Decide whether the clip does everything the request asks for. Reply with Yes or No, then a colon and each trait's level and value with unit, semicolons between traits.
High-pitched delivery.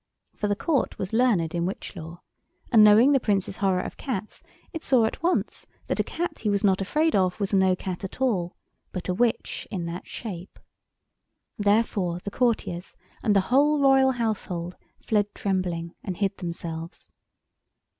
Yes: high, 200 Hz